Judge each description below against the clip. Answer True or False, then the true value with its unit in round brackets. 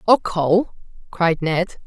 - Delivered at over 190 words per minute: False (130 wpm)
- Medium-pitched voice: True (180 Hz)